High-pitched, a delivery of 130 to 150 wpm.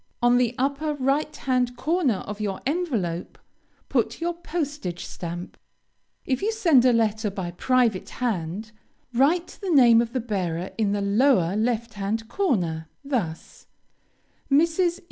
Yes: high, 240 Hz; average, 140 wpm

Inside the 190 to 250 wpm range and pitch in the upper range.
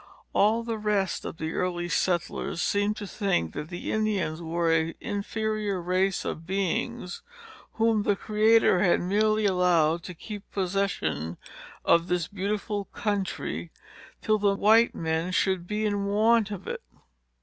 No: average, 145 wpm; high, 195 Hz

